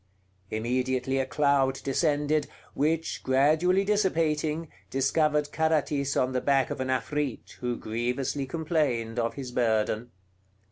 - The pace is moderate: No, slow, 120 wpm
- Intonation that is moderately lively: Yes, average, 3.3 semitones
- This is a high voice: No, medium, 140 Hz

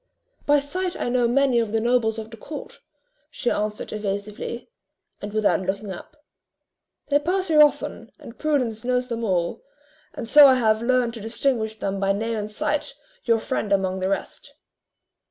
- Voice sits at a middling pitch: No, high, 230 Hz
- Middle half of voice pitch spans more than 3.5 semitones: Yes, average, 4.2 semitones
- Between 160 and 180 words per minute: Yes, average, 175 wpm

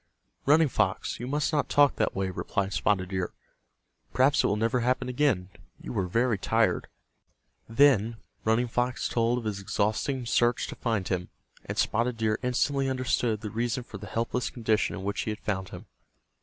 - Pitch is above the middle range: No, low, 115 Hz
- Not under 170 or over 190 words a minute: Yes, average, 180 wpm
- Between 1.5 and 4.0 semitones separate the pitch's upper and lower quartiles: Yes, average, 3.6 semitones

